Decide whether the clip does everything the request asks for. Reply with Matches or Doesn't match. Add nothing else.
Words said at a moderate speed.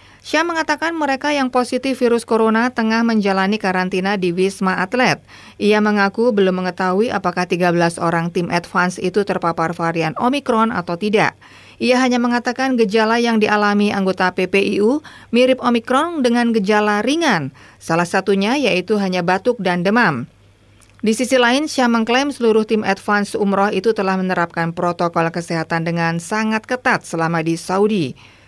Doesn't match